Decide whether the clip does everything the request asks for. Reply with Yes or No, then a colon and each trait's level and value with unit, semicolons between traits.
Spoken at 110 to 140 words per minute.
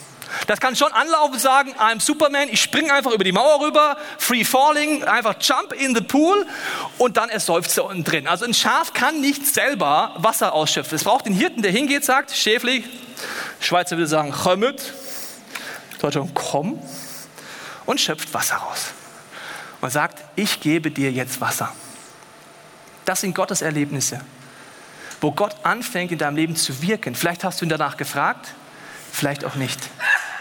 No: average, 160 wpm